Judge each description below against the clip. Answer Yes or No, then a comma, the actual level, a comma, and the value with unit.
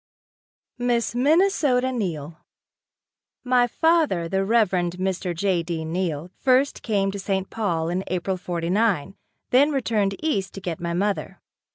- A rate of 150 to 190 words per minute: No, slow, 135 wpm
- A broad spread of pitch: Yes, wide, 5.7 semitones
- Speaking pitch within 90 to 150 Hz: No, high, 195 Hz